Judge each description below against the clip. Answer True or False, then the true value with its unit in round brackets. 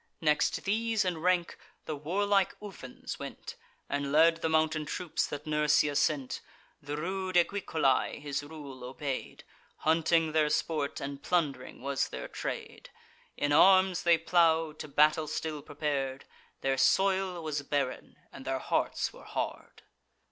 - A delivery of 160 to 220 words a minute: False (140 wpm)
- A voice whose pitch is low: False (155 Hz)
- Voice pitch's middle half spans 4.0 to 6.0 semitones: False (3.2 semitones)